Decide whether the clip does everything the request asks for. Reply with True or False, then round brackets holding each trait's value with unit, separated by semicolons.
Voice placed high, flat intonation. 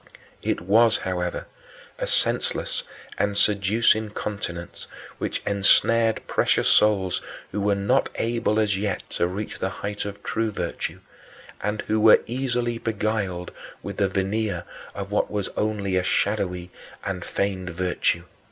False (105 Hz; 2.2 semitones)